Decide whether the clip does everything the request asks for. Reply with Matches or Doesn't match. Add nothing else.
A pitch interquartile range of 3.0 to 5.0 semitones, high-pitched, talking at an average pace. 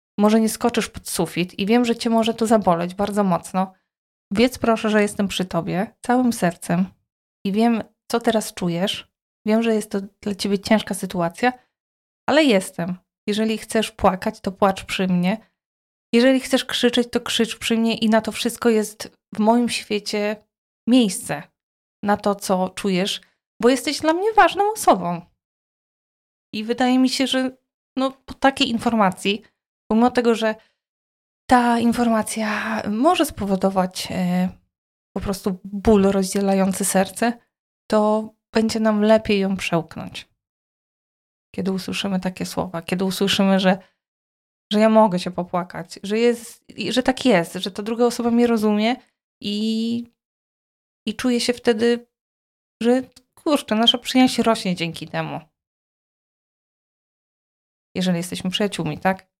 Matches